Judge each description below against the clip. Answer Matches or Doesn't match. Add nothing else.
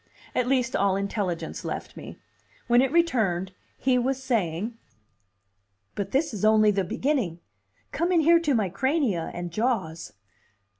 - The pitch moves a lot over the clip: Matches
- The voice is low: Doesn't match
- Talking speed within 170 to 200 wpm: Doesn't match